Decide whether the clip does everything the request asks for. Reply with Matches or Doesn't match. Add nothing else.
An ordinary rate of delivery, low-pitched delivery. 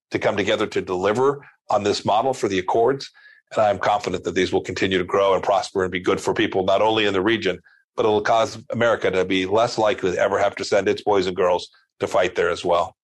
Doesn't match